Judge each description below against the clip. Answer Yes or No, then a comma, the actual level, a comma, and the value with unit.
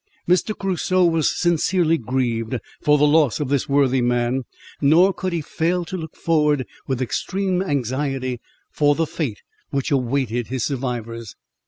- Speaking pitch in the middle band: Yes, medium, 145 Hz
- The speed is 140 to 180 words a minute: Yes, average, 150 wpm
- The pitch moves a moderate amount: Yes, average, 4.7 semitones